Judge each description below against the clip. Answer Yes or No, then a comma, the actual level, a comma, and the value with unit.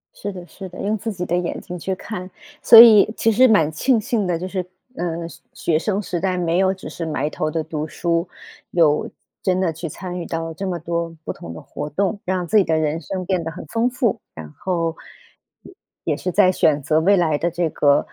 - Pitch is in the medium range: Yes, medium, 180 Hz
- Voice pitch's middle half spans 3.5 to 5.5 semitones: No, average, 3.0 semitones